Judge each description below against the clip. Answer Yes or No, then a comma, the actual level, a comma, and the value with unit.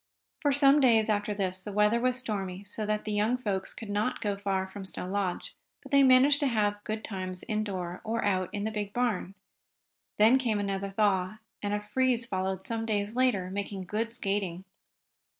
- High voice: Yes, high, 210 Hz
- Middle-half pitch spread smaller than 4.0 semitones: Yes, average, 2.8 semitones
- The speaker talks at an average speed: Yes, average, 190 wpm